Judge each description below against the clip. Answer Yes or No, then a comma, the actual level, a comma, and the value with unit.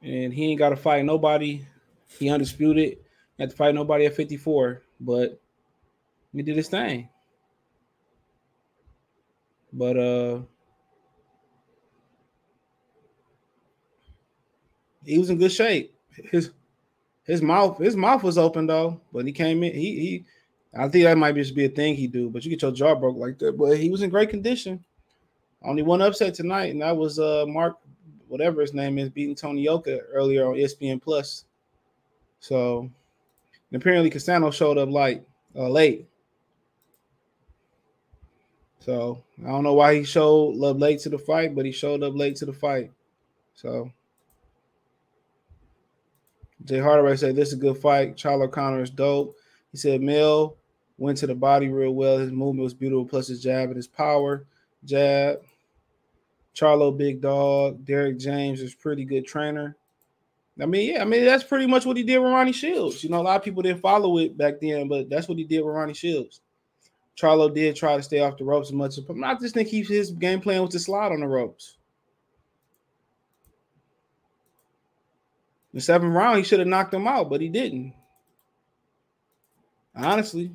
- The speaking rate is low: No, average, 170 wpm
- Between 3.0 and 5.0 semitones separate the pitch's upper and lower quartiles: Yes, average, 3.6 semitones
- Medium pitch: Yes, medium, 145 Hz